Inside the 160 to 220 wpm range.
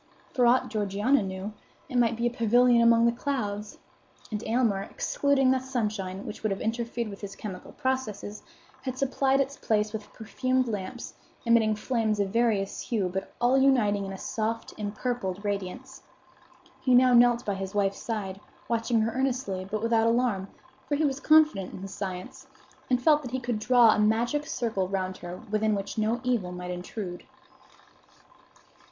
Yes: average, 170 wpm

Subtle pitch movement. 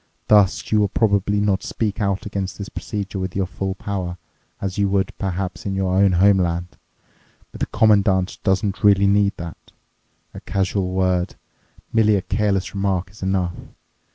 Yes: narrow, 1.4 semitones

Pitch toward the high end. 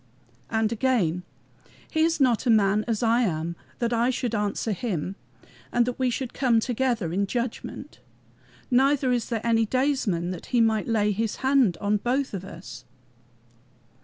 Yes: high, 230 Hz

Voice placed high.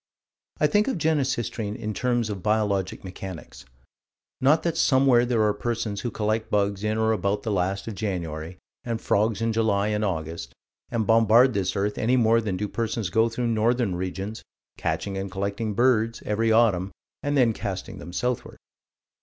No: low, 110 Hz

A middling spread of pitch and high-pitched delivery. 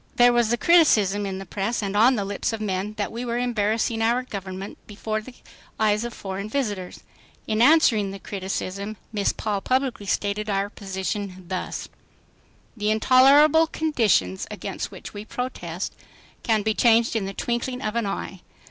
Yes: average, 3.3 semitones; high, 215 Hz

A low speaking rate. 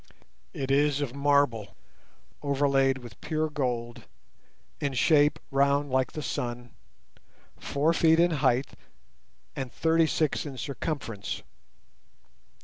Yes: slow, 110 wpm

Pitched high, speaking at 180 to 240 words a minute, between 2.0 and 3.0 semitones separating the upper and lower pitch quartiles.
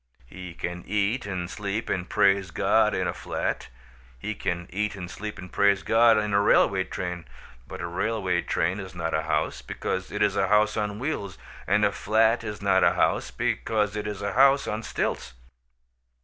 No: low, 100 Hz; average, 190 wpm; narrow, 2.6 semitones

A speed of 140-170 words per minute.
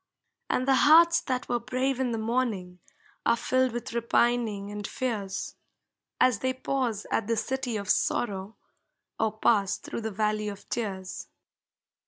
Yes: average, 150 wpm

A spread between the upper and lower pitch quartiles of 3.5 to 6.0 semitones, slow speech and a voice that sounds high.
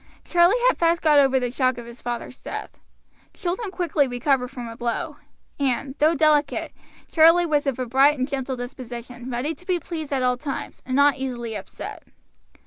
No: average, 4.1 semitones; average, 185 wpm; very high, 270 Hz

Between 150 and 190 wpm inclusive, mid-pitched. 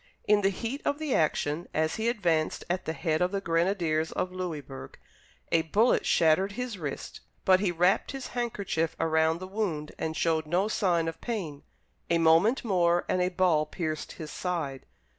Yes: average, 180 wpm; medium, 175 Hz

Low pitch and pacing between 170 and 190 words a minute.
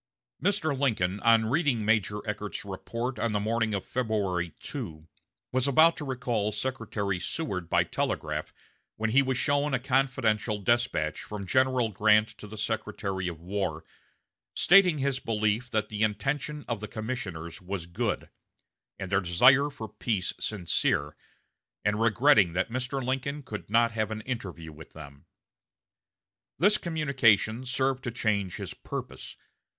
No: low, 110 Hz; average, 145 wpm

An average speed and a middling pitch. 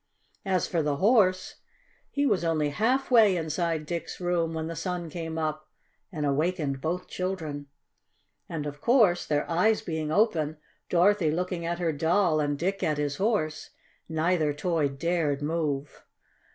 Yes: average, 150 wpm; medium, 165 Hz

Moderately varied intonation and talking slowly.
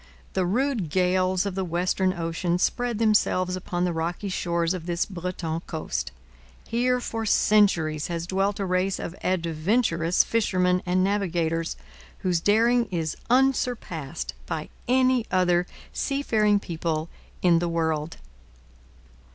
Yes: average, 3.6 semitones; slow, 125 wpm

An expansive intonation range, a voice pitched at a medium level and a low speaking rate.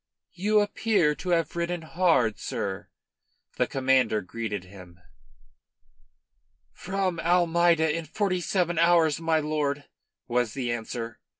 Yes: wide, 6.2 semitones; medium, 160 Hz; slow, 115 wpm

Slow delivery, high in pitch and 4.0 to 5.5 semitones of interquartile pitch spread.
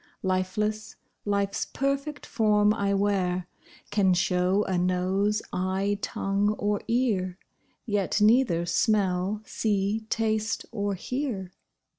No: slow, 105 wpm; high, 205 Hz; narrow, 2.5 semitones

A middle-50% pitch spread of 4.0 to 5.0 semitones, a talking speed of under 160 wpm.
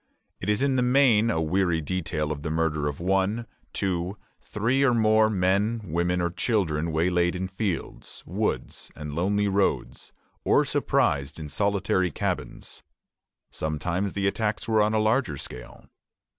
Yes: average, 4.7 semitones; average, 150 wpm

